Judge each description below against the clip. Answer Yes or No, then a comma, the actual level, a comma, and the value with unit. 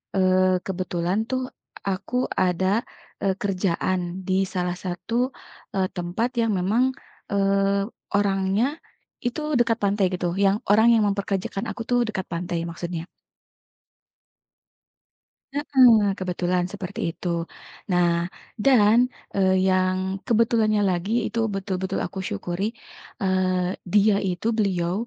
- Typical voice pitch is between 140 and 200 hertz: Yes, high, 190 Hz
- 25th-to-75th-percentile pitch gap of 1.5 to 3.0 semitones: Yes, narrow, 2.5 semitones